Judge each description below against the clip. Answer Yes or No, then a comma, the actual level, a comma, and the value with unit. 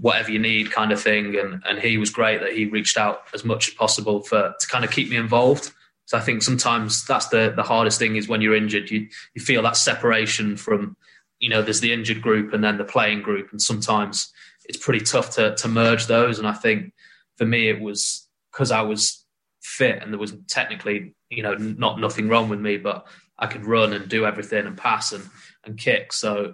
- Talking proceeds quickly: Yes, fast, 225 wpm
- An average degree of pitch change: No, narrow, 1.4 semitones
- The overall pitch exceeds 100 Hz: Yes, low, 110 Hz